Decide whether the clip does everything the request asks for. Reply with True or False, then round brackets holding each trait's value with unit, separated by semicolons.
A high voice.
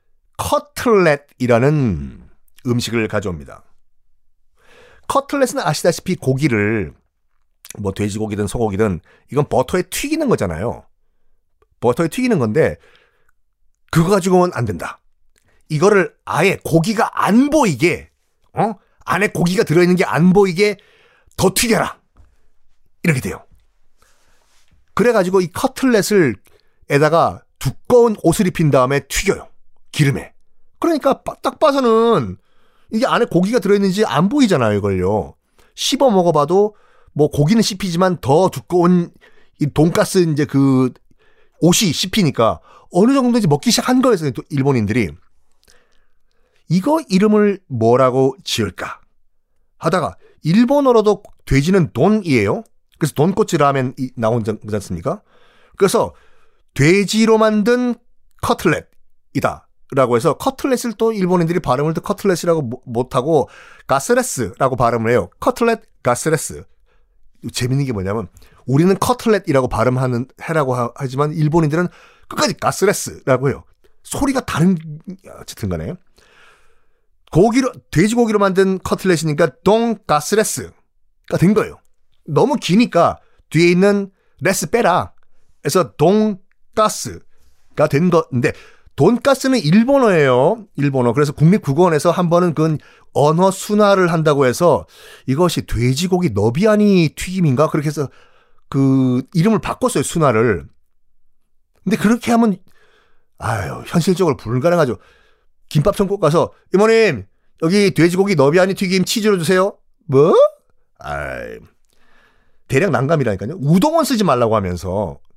False (175 Hz)